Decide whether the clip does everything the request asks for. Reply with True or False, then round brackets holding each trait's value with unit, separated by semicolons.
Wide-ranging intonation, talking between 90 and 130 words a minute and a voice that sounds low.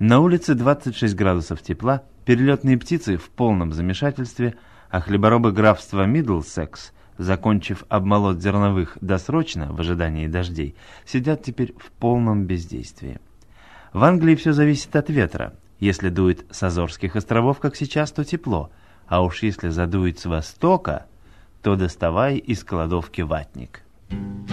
True (5.9 semitones; 125 wpm; 100 Hz)